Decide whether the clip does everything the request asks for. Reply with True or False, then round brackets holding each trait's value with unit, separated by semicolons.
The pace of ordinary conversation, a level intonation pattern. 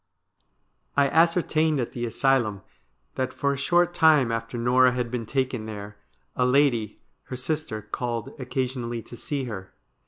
False (160 wpm; 3.4 semitones)